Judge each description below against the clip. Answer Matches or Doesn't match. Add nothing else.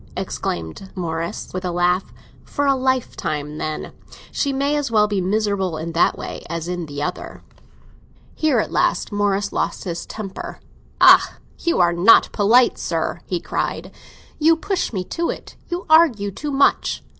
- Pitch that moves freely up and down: Matches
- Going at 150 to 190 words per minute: Matches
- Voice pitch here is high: Matches